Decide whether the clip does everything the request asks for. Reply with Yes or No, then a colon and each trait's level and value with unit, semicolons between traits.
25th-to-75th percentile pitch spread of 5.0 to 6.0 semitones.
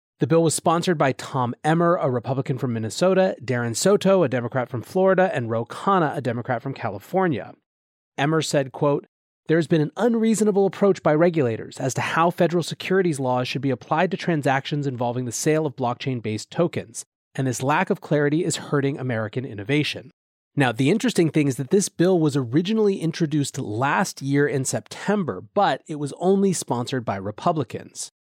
Yes: wide, 5.4 semitones